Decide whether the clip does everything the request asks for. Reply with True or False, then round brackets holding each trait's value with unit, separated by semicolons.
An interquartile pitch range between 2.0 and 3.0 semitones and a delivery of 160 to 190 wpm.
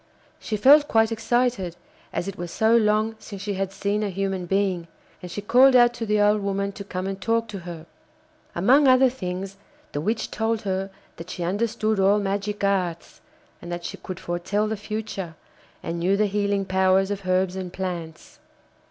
True (2.7 semitones; 185 wpm)